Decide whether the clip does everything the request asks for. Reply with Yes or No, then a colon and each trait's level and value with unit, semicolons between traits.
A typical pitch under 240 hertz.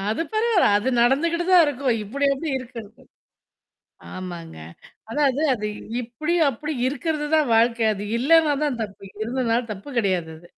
No: very high, 255 Hz